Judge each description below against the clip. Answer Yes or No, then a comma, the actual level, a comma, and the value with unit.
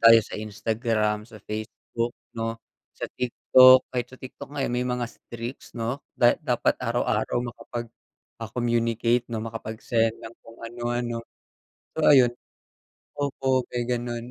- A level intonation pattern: Yes, narrow, 1.4 semitones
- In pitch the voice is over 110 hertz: Yes, low, 120 Hz